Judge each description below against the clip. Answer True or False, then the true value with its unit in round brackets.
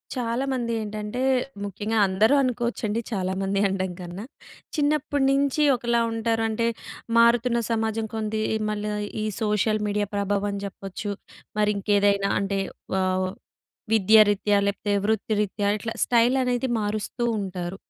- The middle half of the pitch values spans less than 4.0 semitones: True (2.6 semitones)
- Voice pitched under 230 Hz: True (215 Hz)